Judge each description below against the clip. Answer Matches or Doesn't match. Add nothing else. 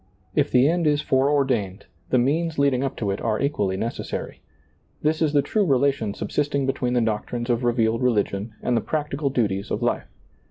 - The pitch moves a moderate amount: Matches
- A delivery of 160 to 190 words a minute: Matches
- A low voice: Matches